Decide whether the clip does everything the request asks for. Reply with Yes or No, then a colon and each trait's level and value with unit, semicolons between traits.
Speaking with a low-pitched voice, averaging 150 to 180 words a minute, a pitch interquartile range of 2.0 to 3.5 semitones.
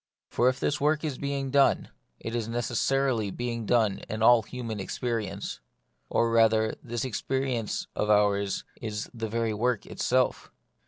Yes: low, 115 Hz; average, 155 wpm; average, 2.8 semitones